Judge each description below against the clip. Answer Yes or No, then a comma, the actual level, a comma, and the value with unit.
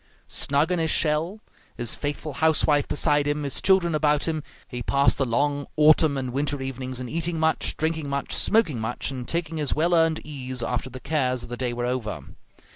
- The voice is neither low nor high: Yes, medium, 145 Hz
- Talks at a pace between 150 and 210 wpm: Yes, average, 200 wpm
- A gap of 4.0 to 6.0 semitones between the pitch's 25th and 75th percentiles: No, average, 3.6 semitones